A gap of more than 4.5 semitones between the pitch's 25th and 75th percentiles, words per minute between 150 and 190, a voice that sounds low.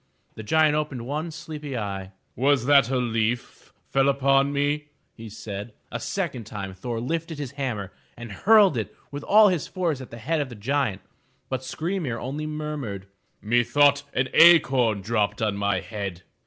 Yes: average, 5.3 semitones; average, 170 wpm; low, 130 Hz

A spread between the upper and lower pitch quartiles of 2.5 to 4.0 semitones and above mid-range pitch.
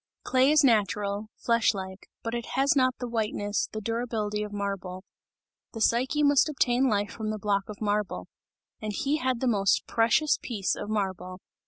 Yes: average, 3.4 semitones; high, 215 Hz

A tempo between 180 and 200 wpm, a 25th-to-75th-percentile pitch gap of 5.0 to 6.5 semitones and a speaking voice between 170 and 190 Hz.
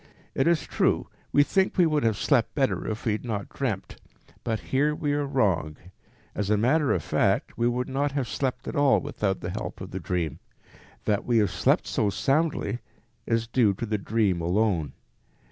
No: average, 195 wpm; wide, 5.4 semitones; low, 115 Hz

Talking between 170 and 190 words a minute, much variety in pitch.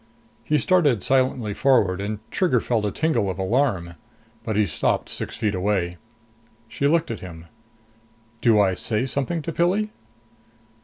No: average, 150 wpm; wide, 6.3 semitones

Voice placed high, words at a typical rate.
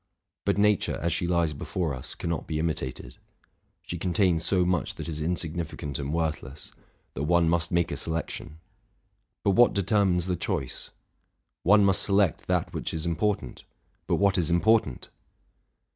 No: very low, 85 Hz; average, 160 wpm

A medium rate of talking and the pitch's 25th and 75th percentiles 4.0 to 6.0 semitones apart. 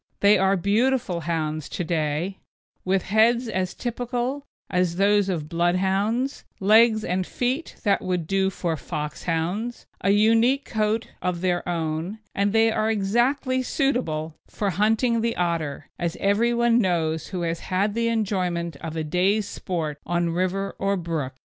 Yes: average, 150 wpm; average, 4.7 semitones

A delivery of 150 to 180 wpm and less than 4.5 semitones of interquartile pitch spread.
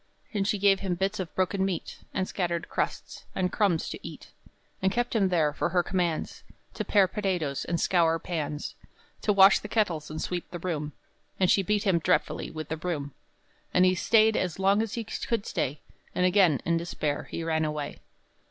No: average, 195 wpm; average, 3.3 semitones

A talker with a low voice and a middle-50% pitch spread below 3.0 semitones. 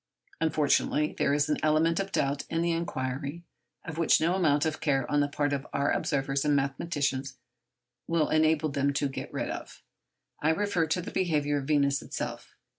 No: medium, 150 Hz; narrow, 2.4 semitones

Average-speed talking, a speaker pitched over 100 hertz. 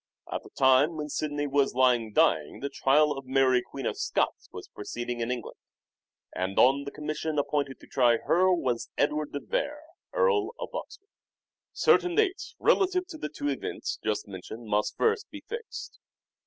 Yes: average, 170 wpm; medium, 140 Hz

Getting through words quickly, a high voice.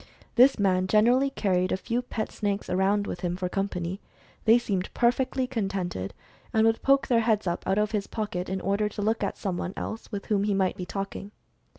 Yes: fast, 220 wpm; high, 200 Hz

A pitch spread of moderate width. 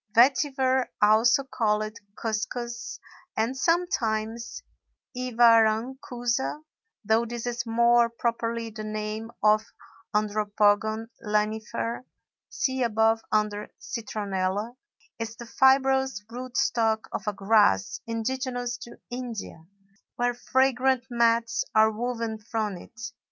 No: narrow, 2.2 semitones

